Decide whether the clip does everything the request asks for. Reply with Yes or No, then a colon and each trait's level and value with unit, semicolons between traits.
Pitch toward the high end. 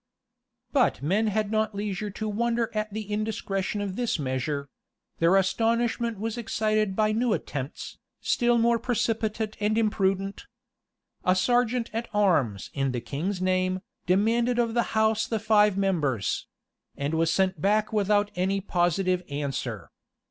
Yes: high, 210 Hz